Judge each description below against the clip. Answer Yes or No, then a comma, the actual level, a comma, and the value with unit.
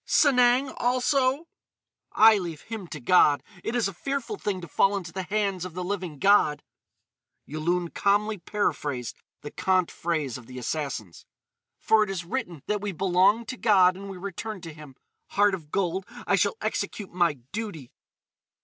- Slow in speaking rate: No, average, 165 wpm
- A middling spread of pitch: Yes, average, 4.4 semitones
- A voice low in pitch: No, high, 190 Hz